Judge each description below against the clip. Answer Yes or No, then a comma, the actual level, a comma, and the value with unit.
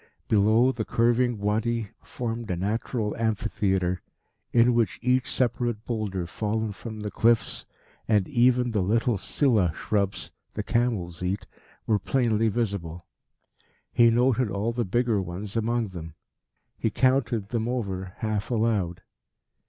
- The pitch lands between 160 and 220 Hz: No, low, 110 Hz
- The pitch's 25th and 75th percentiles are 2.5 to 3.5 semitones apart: Yes, average, 3.1 semitones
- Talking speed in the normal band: No, slow, 130 wpm